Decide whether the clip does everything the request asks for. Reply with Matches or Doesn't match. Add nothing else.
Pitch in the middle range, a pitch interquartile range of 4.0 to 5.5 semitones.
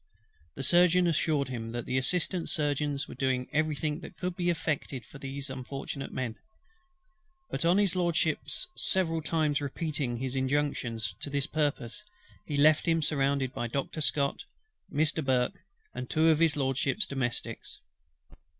Doesn't match